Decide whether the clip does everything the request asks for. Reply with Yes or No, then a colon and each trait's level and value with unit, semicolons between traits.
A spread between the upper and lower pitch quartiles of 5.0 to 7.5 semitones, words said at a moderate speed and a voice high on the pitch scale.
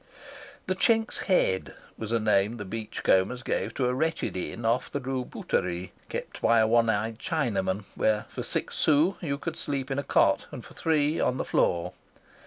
No: average, 5.3 semitones; average, 195 wpm; low, 120 Hz